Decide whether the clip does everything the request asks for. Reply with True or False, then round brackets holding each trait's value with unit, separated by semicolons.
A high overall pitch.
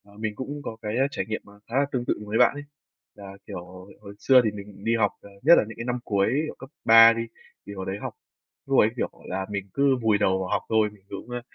False (110 Hz)